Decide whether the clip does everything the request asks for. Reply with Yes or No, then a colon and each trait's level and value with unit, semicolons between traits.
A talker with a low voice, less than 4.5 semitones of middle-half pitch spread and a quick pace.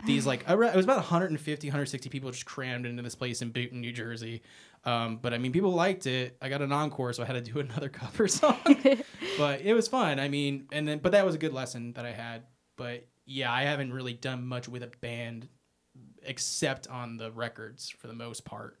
Yes: low, 130 Hz; average, 3.8 semitones; fast, 230 wpm